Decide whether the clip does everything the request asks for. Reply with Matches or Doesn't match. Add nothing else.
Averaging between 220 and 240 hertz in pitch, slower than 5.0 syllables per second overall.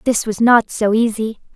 Matches